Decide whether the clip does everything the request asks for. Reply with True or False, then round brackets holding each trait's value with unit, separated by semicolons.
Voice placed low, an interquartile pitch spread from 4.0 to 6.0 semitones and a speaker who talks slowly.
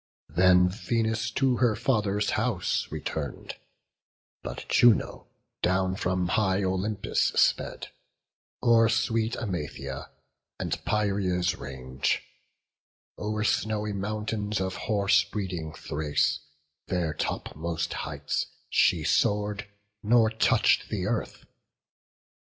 False (100 Hz; 3.2 semitones; 95 wpm)